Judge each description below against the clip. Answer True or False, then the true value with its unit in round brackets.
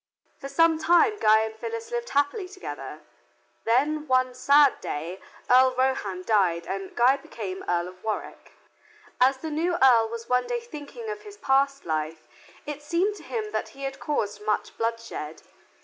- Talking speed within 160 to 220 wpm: True (165 wpm)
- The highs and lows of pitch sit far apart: True (6.9 semitones)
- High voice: True (265 Hz)